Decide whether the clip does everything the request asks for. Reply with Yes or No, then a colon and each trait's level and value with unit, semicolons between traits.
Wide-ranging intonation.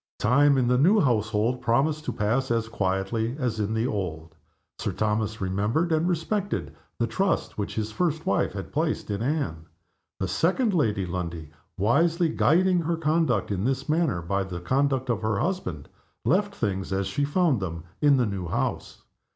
Yes: wide, 7.8 semitones